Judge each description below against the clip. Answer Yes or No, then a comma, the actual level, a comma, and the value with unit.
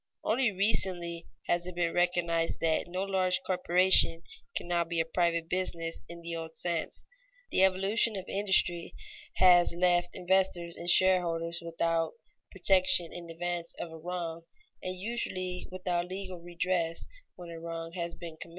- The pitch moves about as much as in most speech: No, narrow, 1.7 semitones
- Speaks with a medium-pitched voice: Yes, medium, 175 Hz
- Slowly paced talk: No, average, 150 wpm